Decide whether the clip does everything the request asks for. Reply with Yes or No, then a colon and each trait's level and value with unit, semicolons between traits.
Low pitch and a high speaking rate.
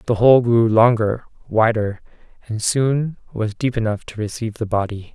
No: low, 115 Hz; average, 165 wpm